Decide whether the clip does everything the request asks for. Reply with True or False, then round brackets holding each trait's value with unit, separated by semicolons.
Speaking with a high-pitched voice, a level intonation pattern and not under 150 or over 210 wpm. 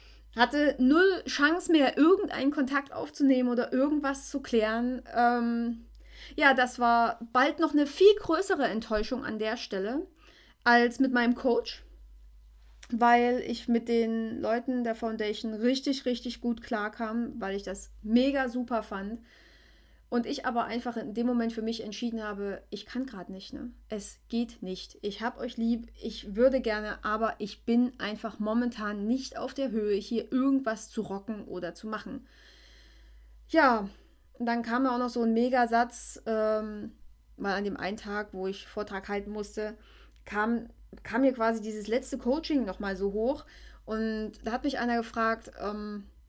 False (235 Hz; 3.0 semitones; 160 wpm)